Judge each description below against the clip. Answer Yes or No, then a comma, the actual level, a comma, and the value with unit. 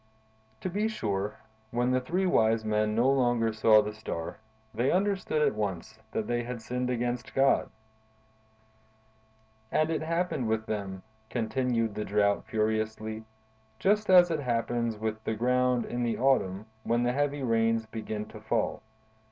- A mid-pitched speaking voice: No, low, 115 Hz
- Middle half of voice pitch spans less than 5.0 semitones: Yes, average, 3.2 semitones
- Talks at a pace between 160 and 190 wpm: No, average, 150 wpm